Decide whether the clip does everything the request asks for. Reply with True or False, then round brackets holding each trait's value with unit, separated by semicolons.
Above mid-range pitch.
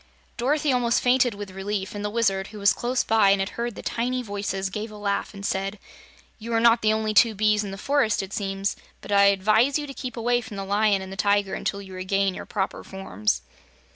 True (205 Hz)